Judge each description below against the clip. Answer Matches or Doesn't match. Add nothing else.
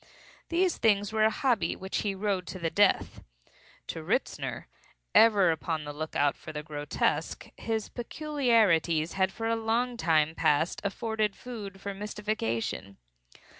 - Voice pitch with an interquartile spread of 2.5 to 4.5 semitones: Doesn't match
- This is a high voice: Matches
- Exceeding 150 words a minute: Doesn't match